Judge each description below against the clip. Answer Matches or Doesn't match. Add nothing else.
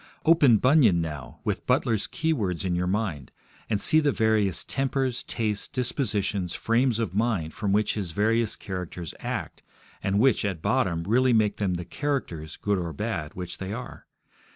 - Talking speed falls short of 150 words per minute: Doesn't match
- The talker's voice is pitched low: Matches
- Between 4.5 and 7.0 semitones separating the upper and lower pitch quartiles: Matches